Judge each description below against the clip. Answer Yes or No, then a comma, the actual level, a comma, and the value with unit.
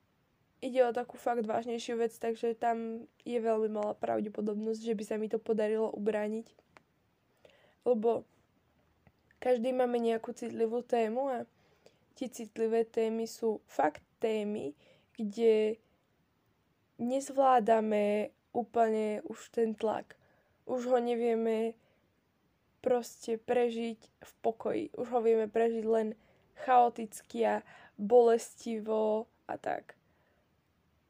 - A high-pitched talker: Yes, high, 230 Hz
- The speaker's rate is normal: No, slow, 105 wpm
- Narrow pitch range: Yes, narrow, 1.4 semitones